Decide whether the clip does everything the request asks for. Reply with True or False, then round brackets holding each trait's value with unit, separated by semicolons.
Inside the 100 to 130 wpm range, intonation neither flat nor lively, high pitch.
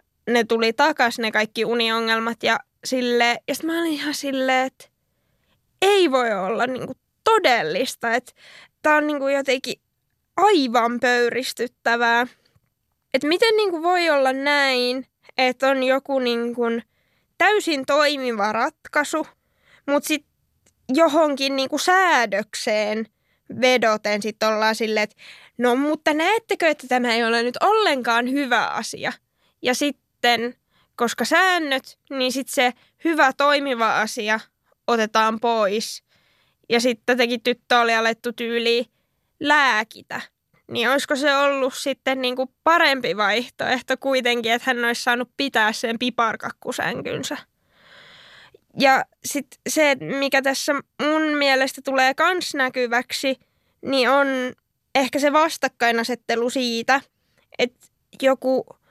True (115 wpm; 3.4 semitones; 260 Hz)